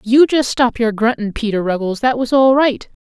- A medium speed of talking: No, fast, 220 wpm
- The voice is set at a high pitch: Yes, high, 235 Hz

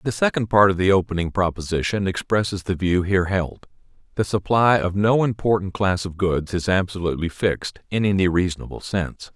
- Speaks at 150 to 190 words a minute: Yes, average, 175 wpm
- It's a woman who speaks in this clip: No, male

